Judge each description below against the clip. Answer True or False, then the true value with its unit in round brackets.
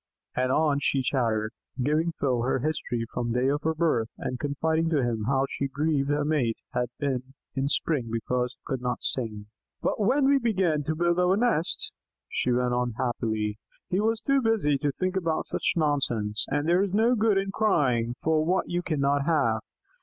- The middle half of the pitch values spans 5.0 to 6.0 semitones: True (5.6 semitones)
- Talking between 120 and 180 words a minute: False (190 wpm)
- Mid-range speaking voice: True (145 Hz)